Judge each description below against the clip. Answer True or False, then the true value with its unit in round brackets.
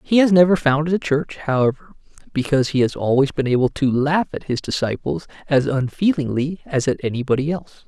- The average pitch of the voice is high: False (145 Hz)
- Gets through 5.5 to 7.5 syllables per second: True (5.8 syllables/s)